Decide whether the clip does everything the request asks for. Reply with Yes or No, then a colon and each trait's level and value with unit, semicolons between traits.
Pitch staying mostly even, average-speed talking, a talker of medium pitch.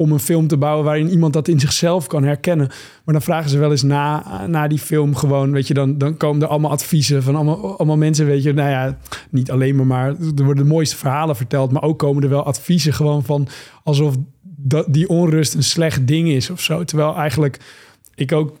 No: narrow, 1.8 semitones; fast, 230 wpm; medium, 150 Hz